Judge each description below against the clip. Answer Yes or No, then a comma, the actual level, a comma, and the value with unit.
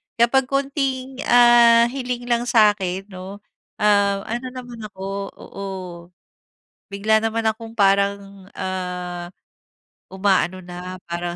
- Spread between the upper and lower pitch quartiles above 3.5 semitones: Yes, average, 4.0 semitones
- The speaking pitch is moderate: No, high, 205 Hz